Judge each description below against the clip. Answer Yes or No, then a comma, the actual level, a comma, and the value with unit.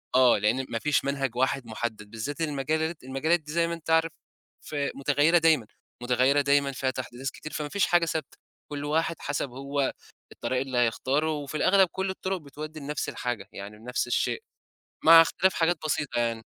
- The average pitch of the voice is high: No, medium, 140 Hz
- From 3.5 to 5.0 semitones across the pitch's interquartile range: Yes, average, 3.8 semitones